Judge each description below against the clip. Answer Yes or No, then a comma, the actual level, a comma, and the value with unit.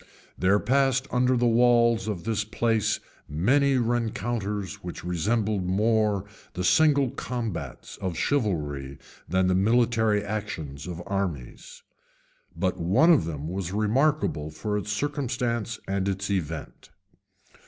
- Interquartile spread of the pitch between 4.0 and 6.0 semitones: Yes, average, 4.6 semitones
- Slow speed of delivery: Yes, slow, 120 wpm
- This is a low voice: Yes, low, 105 Hz